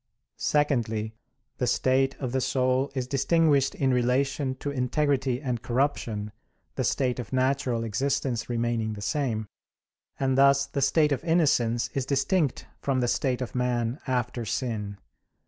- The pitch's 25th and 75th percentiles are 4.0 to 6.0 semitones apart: No, narrow, 2.5 semitones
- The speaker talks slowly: No, average, 145 wpm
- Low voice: Yes, low, 130 Hz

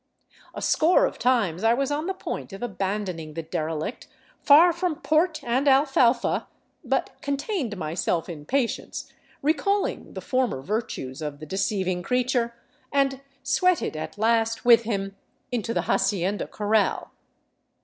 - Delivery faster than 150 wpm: No, average, 140 wpm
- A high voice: Yes, high, 230 Hz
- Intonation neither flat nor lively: No, wide, 6.6 semitones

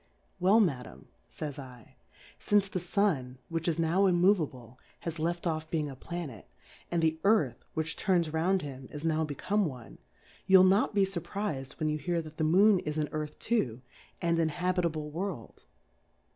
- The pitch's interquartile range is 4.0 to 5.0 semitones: No, average, 3.6 semitones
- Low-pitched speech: No, medium, 165 Hz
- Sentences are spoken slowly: No, average, 170 wpm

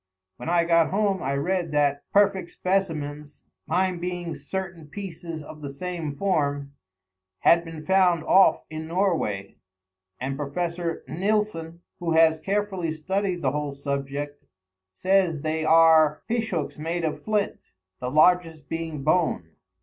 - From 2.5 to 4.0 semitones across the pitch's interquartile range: Yes, average, 3.6 semitones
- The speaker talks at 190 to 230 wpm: No, slow, 135 wpm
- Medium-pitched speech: Yes, medium, 165 Hz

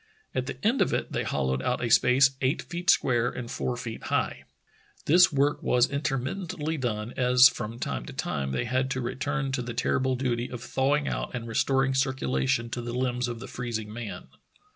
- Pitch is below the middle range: Yes, low, 125 Hz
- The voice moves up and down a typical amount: No, narrow, 2.3 semitones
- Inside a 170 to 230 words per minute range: Yes, average, 195 wpm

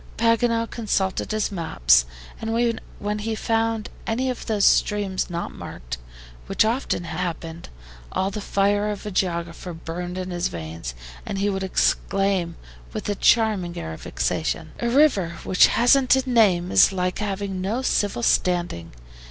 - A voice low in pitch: No, high, 195 Hz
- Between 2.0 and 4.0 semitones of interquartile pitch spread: No, average, 4.4 semitones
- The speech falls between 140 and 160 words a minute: Yes, average, 150 wpm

